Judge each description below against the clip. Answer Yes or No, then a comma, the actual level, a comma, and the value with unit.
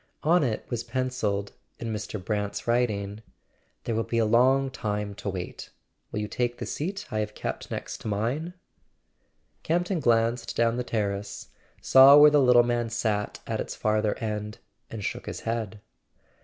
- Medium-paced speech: Yes, average, 170 wpm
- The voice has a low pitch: Yes, low, 115 Hz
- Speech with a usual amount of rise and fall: Yes, average, 3.1 semitones